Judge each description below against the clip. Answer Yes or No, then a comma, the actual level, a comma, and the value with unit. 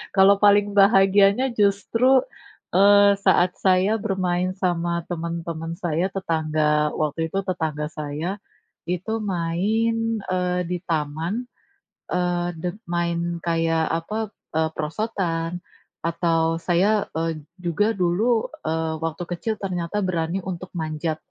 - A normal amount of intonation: Yes, average, 3.2 semitones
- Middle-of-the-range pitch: Yes, medium, 175 Hz